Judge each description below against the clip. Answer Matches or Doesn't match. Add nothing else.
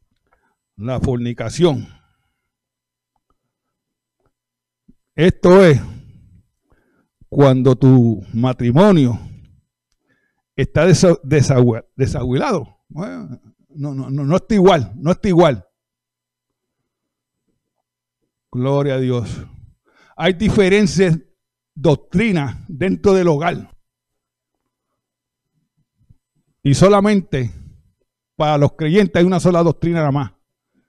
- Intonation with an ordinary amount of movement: Doesn't match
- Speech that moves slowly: Matches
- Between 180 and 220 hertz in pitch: Doesn't match